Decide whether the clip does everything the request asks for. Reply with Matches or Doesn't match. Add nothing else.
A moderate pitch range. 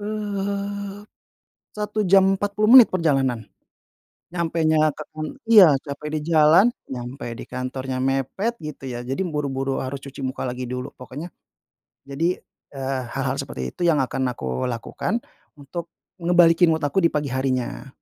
Doesn't match